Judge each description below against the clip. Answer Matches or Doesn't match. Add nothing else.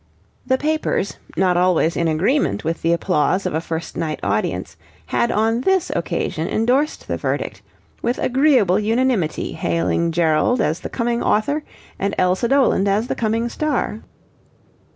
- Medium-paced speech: Matches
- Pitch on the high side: Matches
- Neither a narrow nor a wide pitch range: Doesn't match